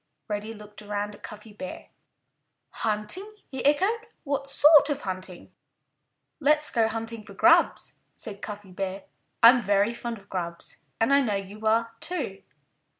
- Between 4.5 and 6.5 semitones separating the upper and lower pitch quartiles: Yes, average, 5.2 semitones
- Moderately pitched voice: No, high, 220 Hz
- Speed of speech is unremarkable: Yes, average, 150 wpm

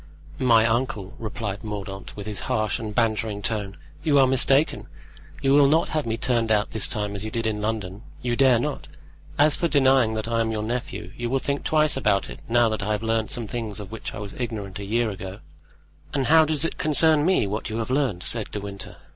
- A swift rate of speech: Yes, fast, 220 wpm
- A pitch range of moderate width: Yes, average, 4.0 semitones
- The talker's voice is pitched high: No, low, 115 Hz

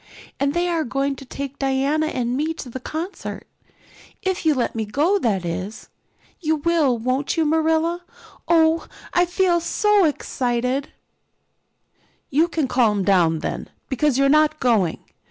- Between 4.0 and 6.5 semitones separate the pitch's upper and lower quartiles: Yes, average, 4.7 semitones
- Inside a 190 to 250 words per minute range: No, average, 150 wpm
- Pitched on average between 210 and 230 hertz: No, very high, 285 Hz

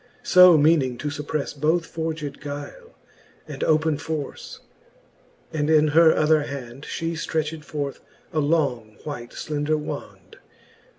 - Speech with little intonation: Yes, narrow, 1.9 semitones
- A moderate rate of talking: No, slow, 125 wpm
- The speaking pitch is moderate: Yes, medium, 150 Hz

